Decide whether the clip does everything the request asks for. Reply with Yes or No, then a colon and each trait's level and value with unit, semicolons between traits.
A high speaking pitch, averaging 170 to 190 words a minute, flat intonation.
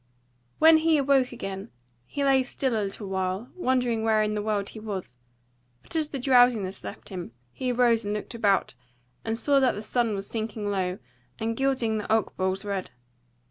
No: high, 220 Hz; average, 180 wpm; average, 4.1 semitones